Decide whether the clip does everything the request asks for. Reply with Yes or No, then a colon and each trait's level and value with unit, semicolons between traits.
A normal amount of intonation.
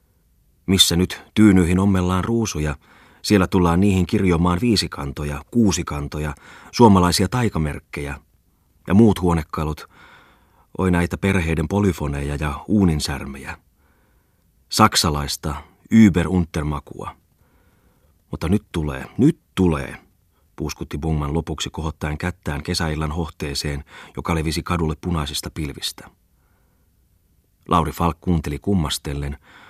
Yes: average, 3.6 semitones